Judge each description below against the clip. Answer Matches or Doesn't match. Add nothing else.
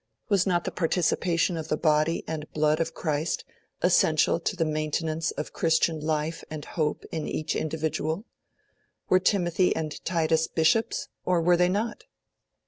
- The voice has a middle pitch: Matches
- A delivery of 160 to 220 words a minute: Doesn't match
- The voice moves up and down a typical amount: Doesn't match